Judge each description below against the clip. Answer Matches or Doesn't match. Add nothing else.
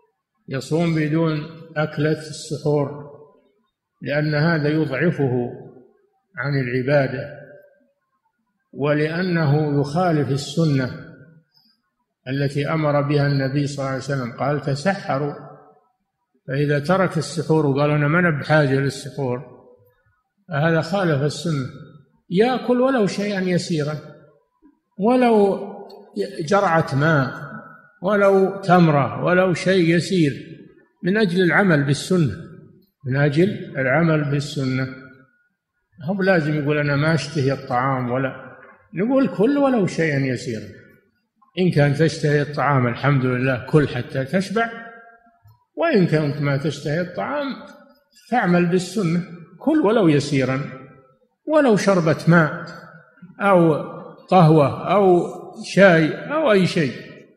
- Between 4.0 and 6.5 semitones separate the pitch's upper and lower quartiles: Matches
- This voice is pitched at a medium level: Matches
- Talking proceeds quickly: Doesn't match